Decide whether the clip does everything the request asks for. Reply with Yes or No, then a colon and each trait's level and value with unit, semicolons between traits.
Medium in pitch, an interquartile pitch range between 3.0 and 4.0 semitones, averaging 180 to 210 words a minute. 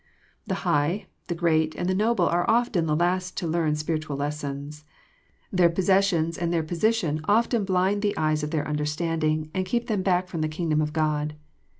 Yes: medium, 165 Hz; average, 3.3 semitones; average, 190 wpm